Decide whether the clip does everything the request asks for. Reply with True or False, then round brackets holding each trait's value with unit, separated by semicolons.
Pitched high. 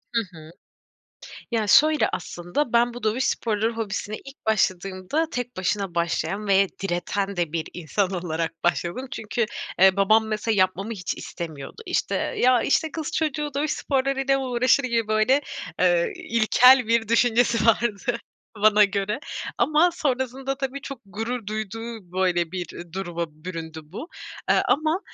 True (220 Hz)